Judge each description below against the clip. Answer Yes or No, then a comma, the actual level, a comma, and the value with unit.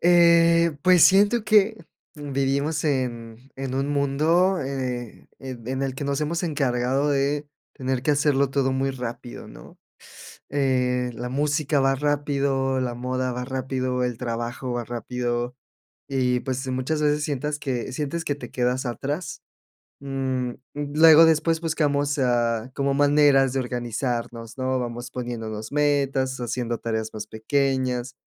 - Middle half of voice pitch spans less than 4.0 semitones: Yes, average, 2.8 semitones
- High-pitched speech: No, low, 135 Hz